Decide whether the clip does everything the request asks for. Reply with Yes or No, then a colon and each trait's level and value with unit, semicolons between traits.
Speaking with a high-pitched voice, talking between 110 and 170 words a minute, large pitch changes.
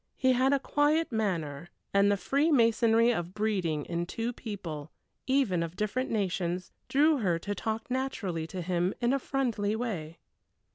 Yes: high, 210 Hz; average, 155 wpm; wide, 6.3 semitones